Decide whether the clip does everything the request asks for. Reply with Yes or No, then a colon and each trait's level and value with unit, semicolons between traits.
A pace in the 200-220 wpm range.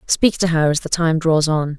No: fast, 270 wpm